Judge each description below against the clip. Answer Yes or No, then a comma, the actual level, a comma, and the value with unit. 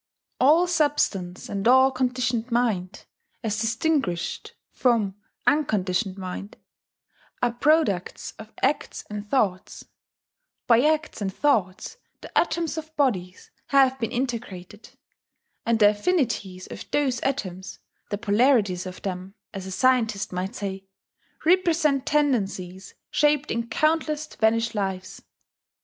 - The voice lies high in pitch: Yes, high, 230 Hz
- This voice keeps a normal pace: No, slow, 115 wpm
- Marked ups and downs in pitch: Yes, wide, 6.2 semitones